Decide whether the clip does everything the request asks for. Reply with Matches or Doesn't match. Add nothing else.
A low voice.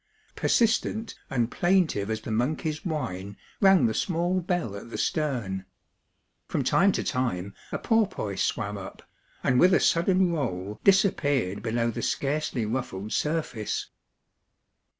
Matches